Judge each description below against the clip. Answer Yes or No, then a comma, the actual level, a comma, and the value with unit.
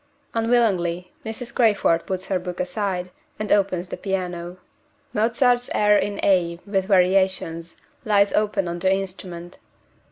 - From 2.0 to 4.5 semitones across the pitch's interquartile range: Yes, average, 2.7 semitones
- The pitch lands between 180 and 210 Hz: Yes, high, 190 Hz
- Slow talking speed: Yes, slow, 130 wpm